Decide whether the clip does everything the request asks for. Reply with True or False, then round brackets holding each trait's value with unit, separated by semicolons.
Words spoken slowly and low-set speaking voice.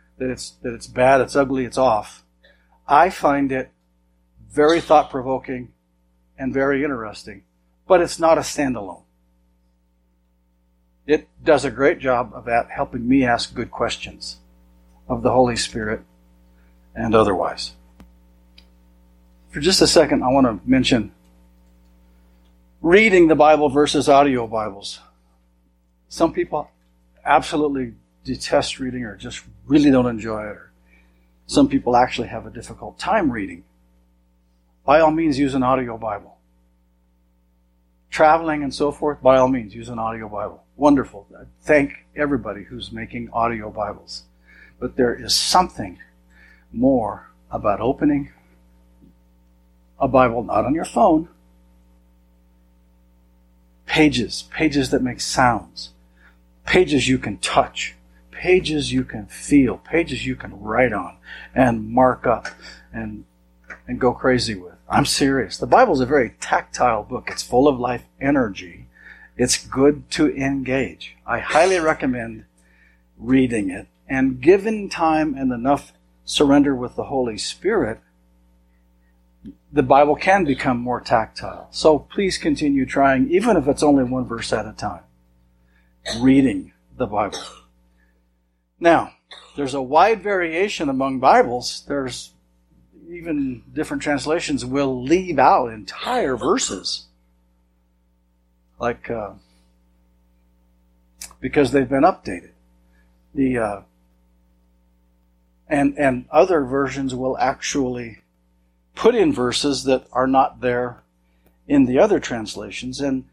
True (125 wpm; 110 Hz)